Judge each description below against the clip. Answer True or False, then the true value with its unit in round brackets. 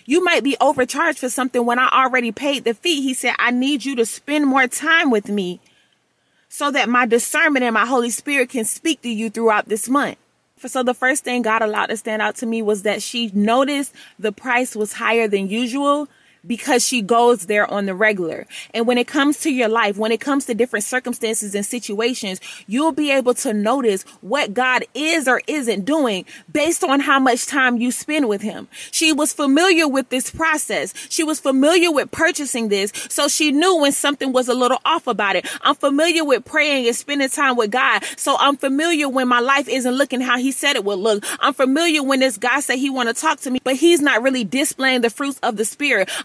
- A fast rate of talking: True (220 wpm)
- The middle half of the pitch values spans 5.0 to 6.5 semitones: False (3.8 semitones)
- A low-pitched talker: False (255 Hz)